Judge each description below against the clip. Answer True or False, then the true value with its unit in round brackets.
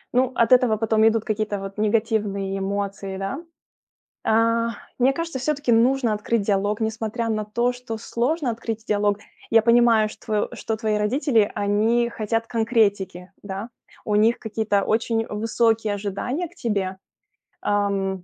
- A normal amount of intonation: False (2.3 semitones)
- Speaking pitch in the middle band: False (220 Hz)